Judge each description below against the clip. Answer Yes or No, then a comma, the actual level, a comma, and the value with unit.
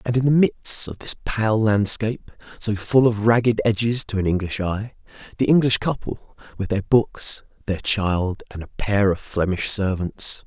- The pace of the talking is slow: No, average, 180 wpm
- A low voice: Yes, low, 105 Hz